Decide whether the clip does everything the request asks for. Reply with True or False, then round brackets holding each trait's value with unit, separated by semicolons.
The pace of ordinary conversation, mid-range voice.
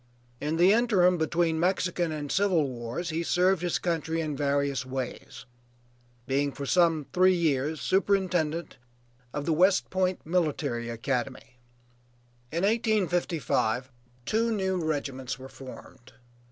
False (125 wpm; 160 Hz)